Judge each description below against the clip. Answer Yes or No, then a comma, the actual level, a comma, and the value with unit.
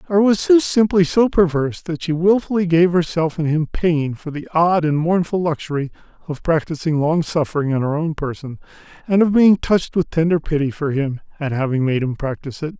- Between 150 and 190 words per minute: No, average, 200 wpm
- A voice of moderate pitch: Yes, medium, 165 Hz